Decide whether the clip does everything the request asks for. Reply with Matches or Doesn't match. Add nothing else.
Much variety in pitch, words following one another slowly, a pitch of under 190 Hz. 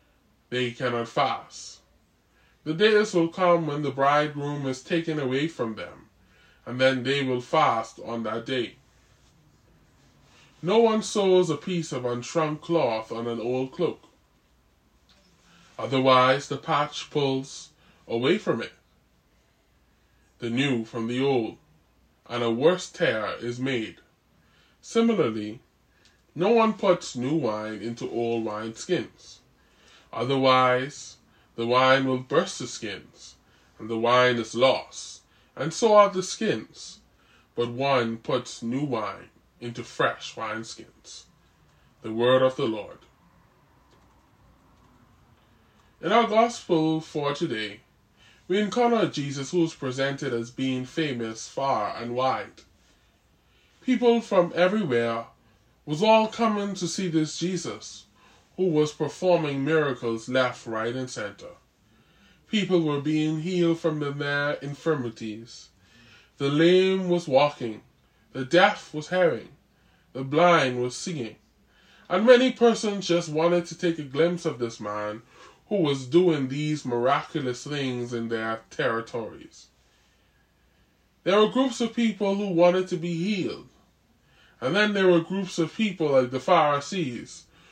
Matches